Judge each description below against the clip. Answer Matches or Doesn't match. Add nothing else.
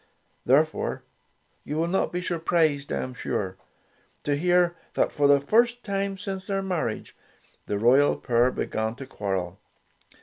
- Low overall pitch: Doesn't match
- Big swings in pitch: Matches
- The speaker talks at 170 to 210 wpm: Doesn't match